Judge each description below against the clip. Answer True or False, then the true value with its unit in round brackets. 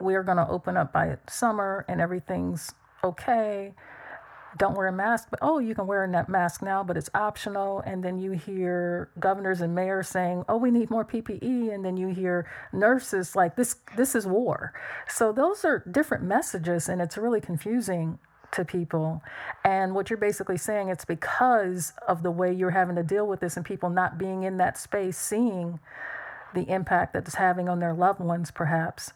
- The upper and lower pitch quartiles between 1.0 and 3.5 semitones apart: True (2.8 semitones)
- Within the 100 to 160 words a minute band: False (200 wpm)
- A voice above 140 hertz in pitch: True (190 Hz)